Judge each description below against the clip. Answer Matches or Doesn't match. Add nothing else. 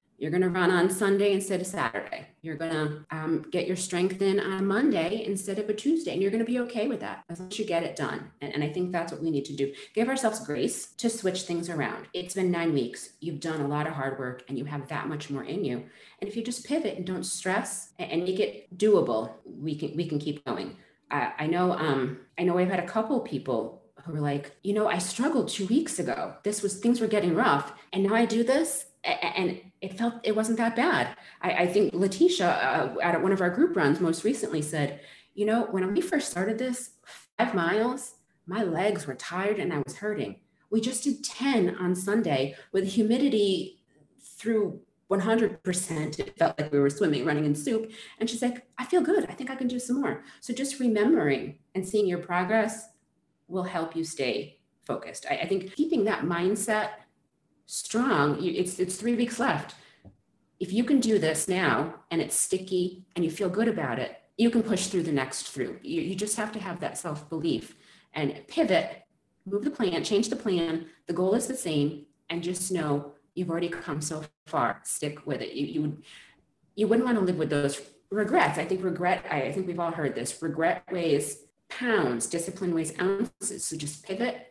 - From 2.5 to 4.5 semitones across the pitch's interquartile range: Doesn't match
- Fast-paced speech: Matches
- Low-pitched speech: Doesn't match